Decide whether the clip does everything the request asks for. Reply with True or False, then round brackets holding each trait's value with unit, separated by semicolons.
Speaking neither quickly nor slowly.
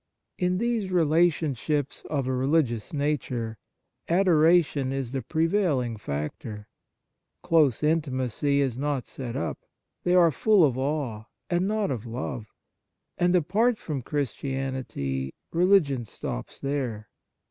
False (115 wpm)